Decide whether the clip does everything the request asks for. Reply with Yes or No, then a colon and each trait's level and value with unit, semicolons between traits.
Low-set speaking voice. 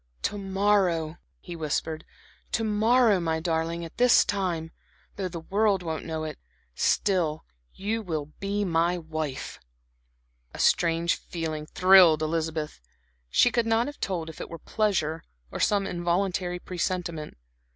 No: medium, 175 Hz